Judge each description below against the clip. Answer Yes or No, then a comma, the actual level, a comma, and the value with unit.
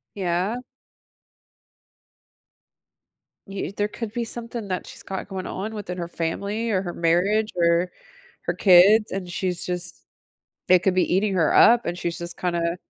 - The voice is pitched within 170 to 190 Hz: Yes, medium, 185 Hz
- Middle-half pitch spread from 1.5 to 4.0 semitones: Yes, average, 3.1 semitones